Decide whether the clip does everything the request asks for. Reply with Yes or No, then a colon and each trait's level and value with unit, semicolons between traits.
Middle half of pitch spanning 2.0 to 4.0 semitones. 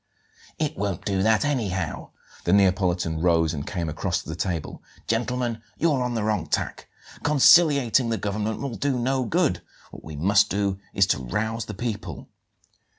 No: average, 5.3 semitones